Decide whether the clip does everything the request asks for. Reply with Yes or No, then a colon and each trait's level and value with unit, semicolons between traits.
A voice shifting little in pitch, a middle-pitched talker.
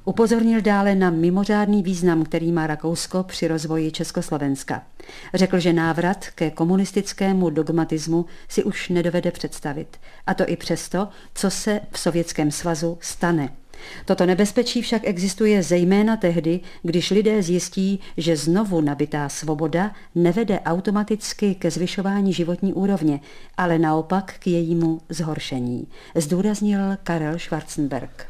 No: average, 3.1 semitones; medium, 175 Hz